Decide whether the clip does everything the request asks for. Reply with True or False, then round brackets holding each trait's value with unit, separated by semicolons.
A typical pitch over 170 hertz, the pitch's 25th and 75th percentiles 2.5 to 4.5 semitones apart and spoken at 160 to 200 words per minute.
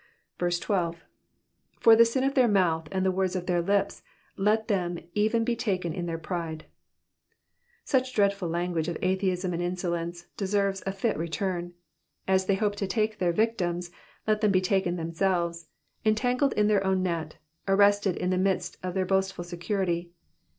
True (190 Hz; 2.8 semitones; 170 wpm)